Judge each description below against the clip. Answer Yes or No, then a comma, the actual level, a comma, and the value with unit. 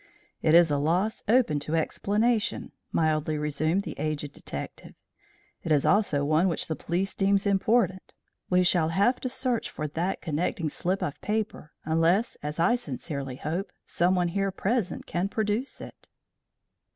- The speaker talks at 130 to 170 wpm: Yes, average, 150 wpm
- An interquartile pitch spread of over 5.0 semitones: No, average, 4.5 semitones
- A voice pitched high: No, medium, 175 Hz